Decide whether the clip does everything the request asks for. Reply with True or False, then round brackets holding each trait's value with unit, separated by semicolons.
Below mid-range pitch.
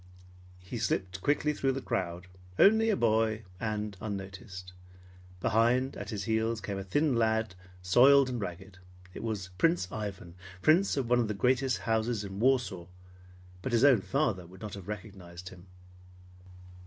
True (110 Hz)